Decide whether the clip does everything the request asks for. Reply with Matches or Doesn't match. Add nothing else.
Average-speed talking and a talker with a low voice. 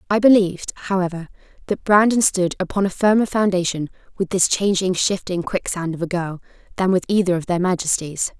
Doesn't match